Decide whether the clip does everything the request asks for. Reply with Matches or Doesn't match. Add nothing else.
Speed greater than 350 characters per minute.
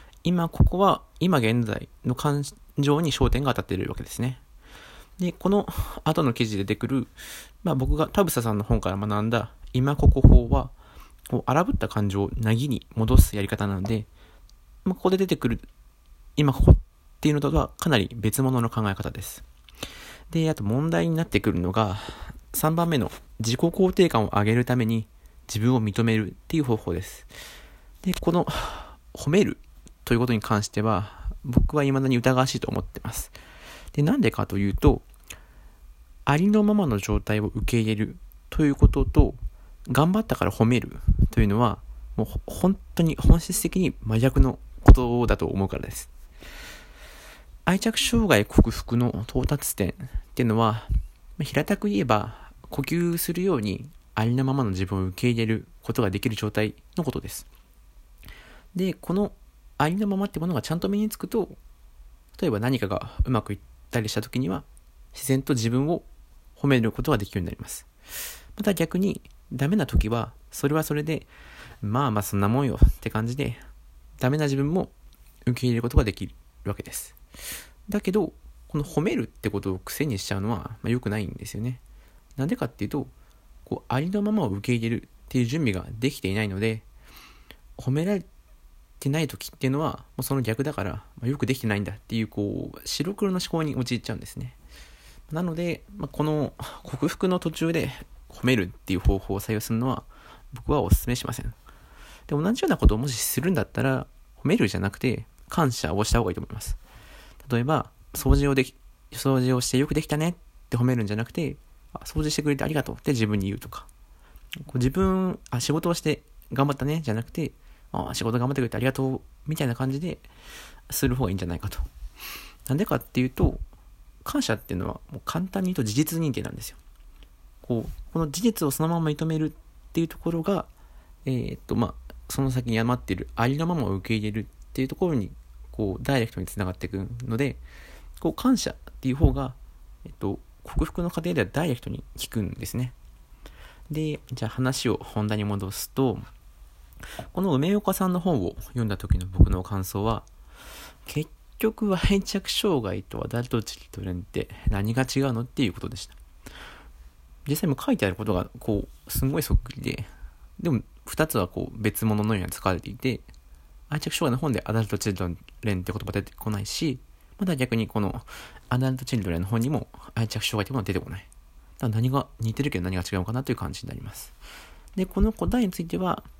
Matches